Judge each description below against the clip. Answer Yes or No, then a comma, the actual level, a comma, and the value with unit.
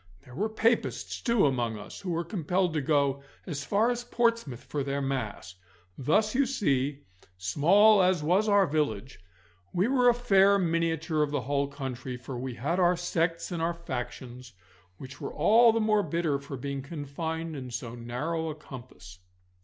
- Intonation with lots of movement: Yes, wide, 6.3 semitones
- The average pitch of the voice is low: No, medium, 155 Hz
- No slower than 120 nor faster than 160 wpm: No, average, 175 wpm